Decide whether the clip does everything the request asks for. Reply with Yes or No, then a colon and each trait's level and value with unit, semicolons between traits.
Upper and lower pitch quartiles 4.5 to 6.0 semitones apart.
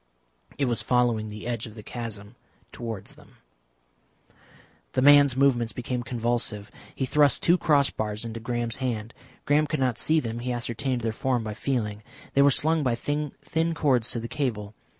No: average, 3.7 semitones